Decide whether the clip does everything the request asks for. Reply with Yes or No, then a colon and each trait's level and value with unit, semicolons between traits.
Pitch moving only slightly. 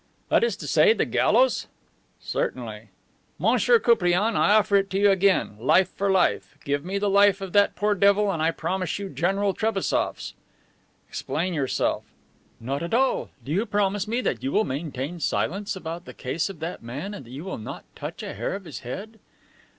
No: average, 4.2 semitones